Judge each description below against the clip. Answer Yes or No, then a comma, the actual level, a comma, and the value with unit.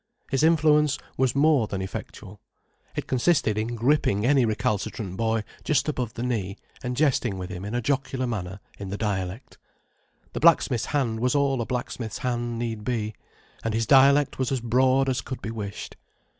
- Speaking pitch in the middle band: No, low, 120 Hz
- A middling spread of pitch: Yes, average, 3.9 semitones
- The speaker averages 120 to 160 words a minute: No, average, 175 wpm